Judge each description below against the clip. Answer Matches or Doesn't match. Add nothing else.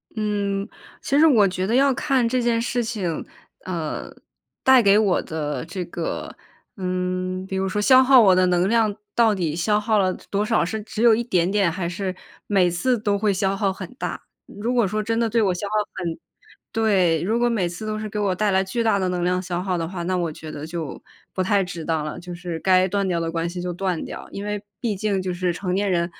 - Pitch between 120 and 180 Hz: Doesn't match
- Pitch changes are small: Doesn't match